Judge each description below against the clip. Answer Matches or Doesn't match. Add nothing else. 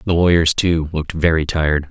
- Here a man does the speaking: Matches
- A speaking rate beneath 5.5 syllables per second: Doesn't match